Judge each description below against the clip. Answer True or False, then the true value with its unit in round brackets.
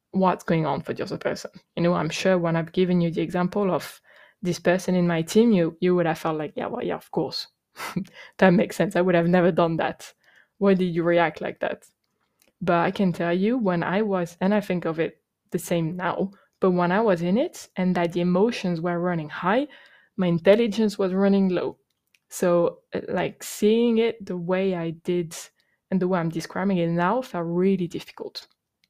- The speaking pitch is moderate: True (180 Hz)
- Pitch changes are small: True (2.3 semitones)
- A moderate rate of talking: False (210 wpm)